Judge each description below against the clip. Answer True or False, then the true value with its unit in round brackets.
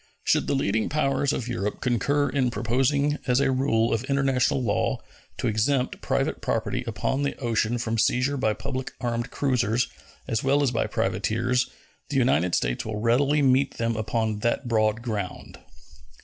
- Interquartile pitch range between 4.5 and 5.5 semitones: False (3.4 semitones)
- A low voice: True (120 Hz)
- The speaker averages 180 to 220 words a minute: False (165 wpm)